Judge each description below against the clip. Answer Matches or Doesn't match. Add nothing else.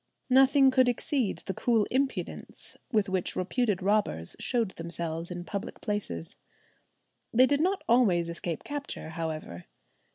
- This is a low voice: Doesn't match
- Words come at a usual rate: Doesn't match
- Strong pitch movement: Matches